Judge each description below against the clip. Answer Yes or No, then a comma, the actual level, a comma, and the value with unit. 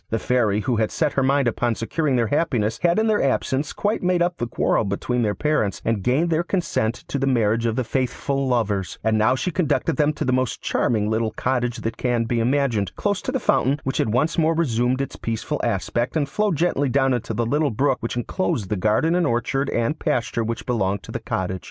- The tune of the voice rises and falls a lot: No, average, 4.7 semitones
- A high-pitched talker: No, low, 125 Hz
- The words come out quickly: Yes, fast, 225 wpm